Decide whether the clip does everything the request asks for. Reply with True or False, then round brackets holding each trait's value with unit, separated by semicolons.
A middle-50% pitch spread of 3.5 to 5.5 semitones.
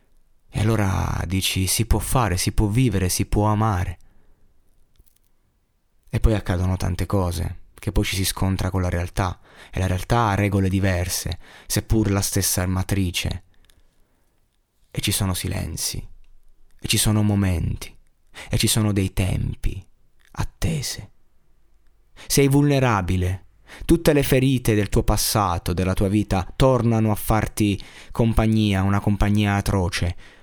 False (2.8 semitones)